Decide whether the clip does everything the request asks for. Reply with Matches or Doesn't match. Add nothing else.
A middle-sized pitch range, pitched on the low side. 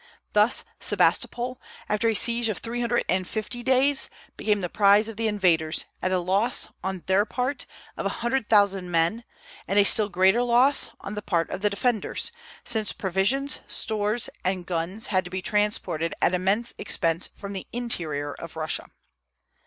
Doesn't match